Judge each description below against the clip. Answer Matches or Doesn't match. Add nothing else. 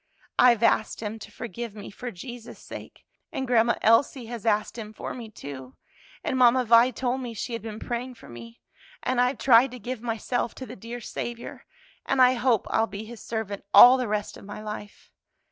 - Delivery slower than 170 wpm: Doesn't match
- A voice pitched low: Doesn't match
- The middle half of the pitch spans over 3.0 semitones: Doesn't match